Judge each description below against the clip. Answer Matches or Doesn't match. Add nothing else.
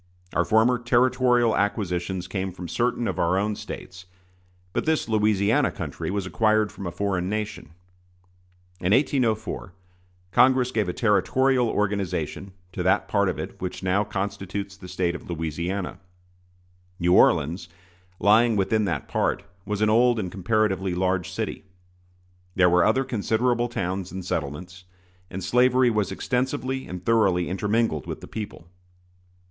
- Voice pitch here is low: Matches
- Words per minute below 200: Matches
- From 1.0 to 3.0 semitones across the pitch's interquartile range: Doesn't match